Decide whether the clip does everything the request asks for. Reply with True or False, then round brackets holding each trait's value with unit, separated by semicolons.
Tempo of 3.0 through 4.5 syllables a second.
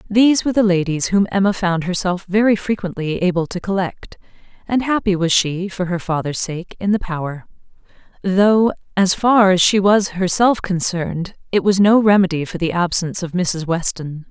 False (5.1 syllables/s)